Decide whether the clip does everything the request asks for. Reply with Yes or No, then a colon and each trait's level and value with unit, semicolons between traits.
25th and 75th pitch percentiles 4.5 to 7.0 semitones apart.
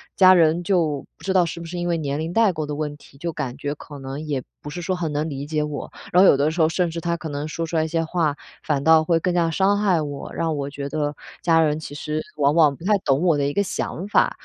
No: average, 2.8 semitones